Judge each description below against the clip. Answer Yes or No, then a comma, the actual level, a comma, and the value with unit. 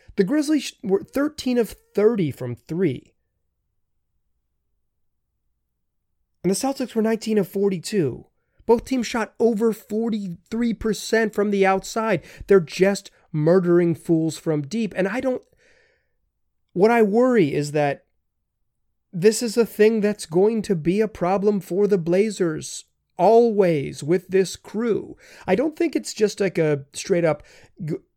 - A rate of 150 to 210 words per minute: No, slow, 135 wpm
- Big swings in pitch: Yes, wide, 5.7 semitones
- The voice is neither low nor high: No, high, 195 Hz